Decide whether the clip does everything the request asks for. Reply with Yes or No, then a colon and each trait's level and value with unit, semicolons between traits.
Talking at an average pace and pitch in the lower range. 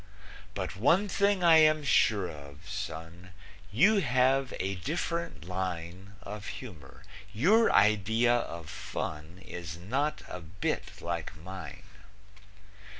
No: slow, 115 wpm; low, 100 Hz